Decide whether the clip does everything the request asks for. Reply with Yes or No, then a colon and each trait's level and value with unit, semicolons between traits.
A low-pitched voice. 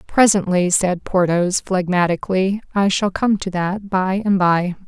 No: high, 190 Hz